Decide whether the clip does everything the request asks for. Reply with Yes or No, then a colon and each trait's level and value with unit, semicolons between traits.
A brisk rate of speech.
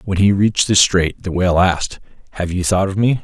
Yes: fast, 240 wpm